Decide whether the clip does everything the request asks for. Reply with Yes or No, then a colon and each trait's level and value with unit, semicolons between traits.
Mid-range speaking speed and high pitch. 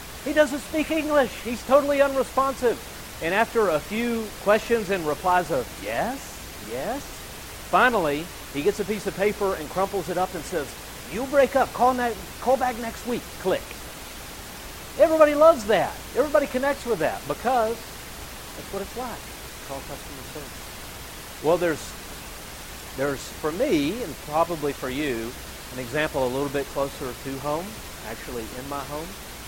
Yes: average, 155 wpm; high, 205 Hz